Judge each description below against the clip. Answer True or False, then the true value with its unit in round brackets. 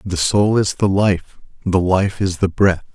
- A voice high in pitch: False (95 Hz)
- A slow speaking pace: False (205 wpm)